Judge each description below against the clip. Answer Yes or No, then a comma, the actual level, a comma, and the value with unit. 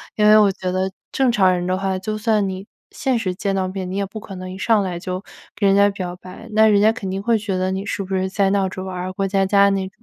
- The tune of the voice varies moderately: No, narrow, 1.8 semitones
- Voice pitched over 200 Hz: No, high, 195 Hz